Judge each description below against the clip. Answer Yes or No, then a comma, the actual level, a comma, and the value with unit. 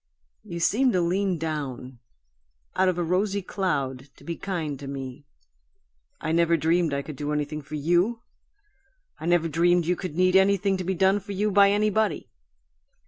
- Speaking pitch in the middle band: Yes, medium, 175 Hz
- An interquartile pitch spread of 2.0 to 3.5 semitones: No, average, 4.1 semitones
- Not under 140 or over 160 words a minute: No, average, 175 wpm